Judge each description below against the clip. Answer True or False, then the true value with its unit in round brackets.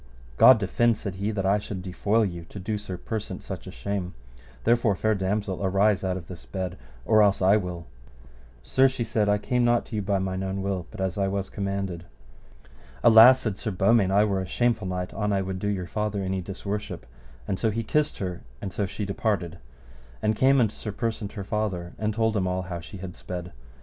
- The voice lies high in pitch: False (100 Hz)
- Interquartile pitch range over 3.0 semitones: False (2.6 semitones)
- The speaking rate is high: True (215 wpm)